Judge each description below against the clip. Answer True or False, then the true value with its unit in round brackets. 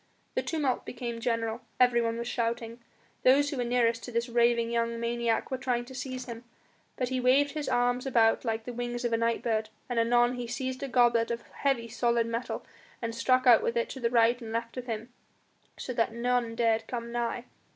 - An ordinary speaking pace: False (210 wpm)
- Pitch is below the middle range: False (235 Hz)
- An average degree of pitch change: False (1.3 semitones)